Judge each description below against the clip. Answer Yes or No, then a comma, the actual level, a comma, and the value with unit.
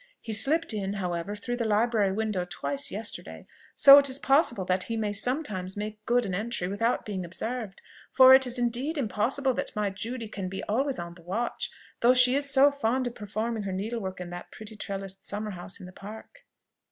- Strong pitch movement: No, average, 4.2 semitones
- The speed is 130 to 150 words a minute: No, average, 200 wpm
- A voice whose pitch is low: No, high, 220 Hz